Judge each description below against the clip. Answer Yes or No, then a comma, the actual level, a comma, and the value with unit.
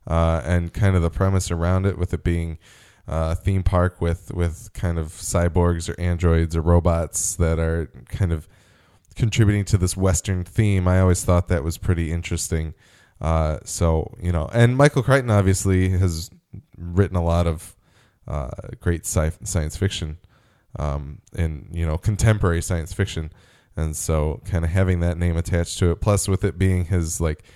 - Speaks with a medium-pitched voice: No, very low, 90 Hz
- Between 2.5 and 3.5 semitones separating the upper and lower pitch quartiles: Yes, average, 2.8 semitones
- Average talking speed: Yes, average, 175 wpm